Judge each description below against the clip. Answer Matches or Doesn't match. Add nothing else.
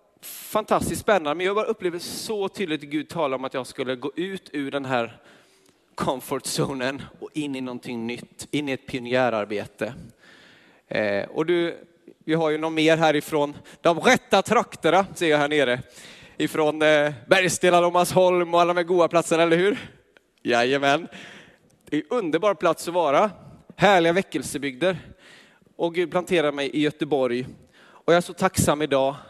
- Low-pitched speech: Doesn't match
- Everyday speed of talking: Matches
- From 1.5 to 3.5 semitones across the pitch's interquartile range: Doesn't match